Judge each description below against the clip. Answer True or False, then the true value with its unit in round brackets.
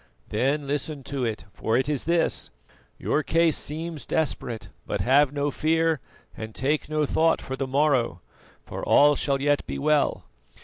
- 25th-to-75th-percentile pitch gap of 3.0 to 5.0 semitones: False (2.6 semitones)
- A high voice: False (145 Hz)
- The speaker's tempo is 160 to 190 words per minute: True (165 wpm)